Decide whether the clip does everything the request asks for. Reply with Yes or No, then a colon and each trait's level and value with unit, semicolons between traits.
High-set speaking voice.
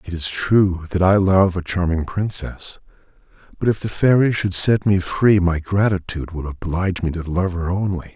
No: very low, 90 Hz